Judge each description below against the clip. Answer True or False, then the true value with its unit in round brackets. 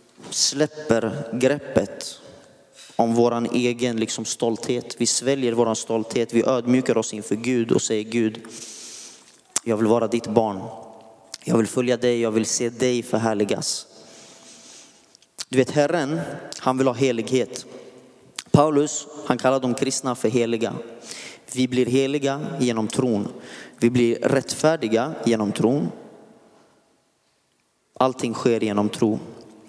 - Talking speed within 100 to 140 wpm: True (125 wpm)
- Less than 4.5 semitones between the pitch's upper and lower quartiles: True (2.5 semitones)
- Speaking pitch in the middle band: False (120 Hz)